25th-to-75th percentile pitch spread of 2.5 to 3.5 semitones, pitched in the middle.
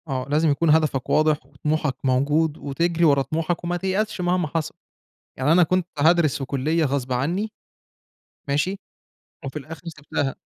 Yes: average, 3.2 semitones; medium, 155 Hz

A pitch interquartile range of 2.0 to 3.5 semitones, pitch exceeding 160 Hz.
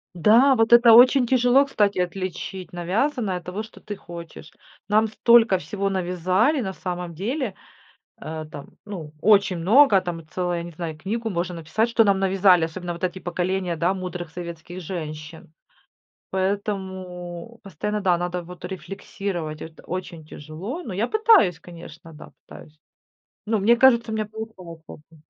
No: average, 4.1 semitones; medium, 185 Hz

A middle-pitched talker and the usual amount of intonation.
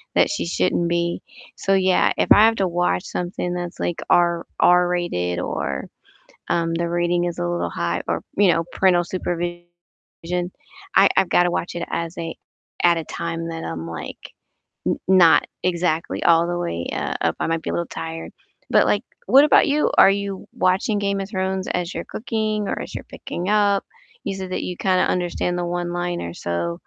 No: medium, 175 Hz; narrow, 2.1 semitones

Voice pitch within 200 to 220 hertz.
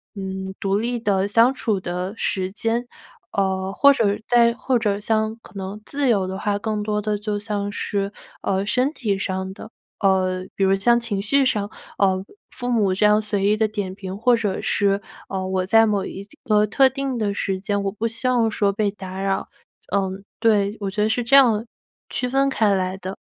Yes: high, 205 Hz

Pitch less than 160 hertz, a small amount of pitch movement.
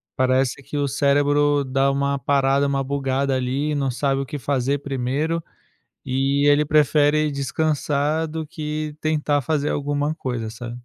Yes: medium, 140 Hz; narrow, 1.7 semitones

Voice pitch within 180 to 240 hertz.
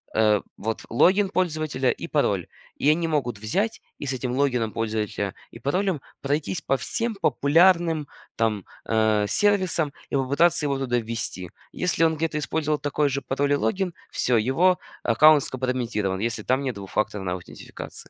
No: low, 135 Hz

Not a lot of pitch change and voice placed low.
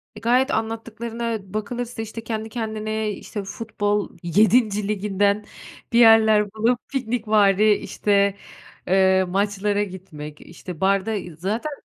No: narrow, 2.1 semitones; high, 210 Hz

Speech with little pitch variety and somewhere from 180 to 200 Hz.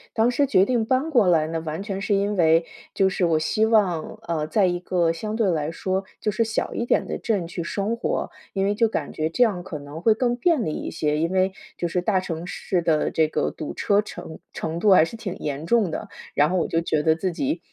No: average, 4.8 semitones; medium, 185 Hz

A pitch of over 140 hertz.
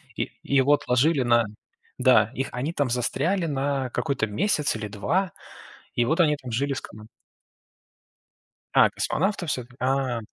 No: low, 135 Hz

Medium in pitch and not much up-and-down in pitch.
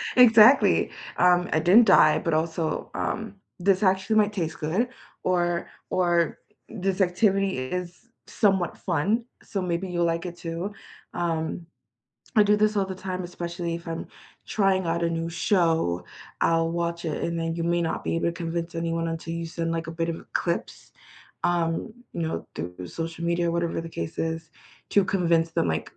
Yes: medium, 170 Hz; narrow, 2.2 semitones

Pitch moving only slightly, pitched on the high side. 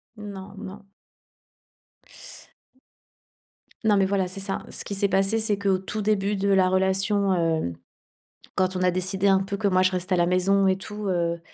Yes: narrow, 1.3 semitones; high, 195 Hz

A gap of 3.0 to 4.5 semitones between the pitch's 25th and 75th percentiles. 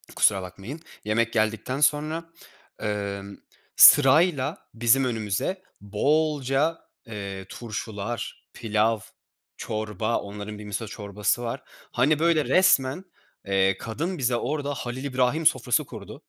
No: average, 5.3 semitones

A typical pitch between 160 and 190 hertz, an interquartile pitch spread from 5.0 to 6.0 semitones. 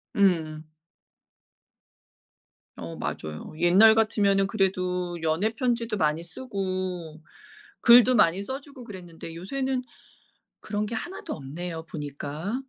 Yes: medium, 185 Hz; average, 5.3 semitones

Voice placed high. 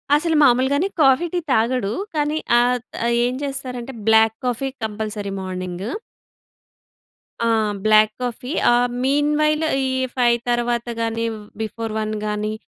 Yes: high, 240 Hz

